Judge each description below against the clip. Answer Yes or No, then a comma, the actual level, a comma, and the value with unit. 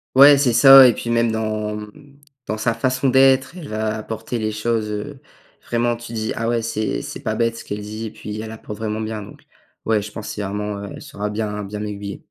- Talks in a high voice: No, low, 110 Hz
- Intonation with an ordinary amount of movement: No, narrow, 2.0 semitones